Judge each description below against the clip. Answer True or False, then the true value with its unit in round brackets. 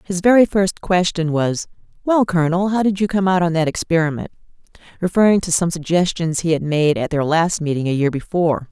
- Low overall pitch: False (170 Hz)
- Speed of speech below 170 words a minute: False (195 wpm)